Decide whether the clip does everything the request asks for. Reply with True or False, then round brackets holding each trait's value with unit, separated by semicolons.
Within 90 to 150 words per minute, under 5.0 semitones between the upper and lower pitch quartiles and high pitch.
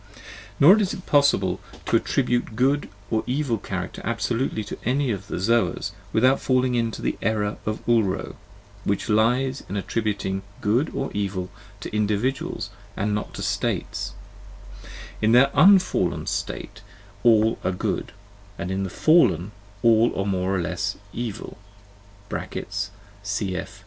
False (140 wpm; 3.8 semitones; 110 Hz)